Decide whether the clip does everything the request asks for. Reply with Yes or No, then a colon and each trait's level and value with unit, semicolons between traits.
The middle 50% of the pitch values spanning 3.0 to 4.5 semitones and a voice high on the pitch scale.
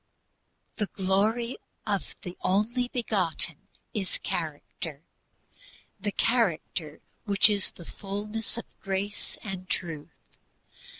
Yes: average, 3.4 semitones; high, 195 Hz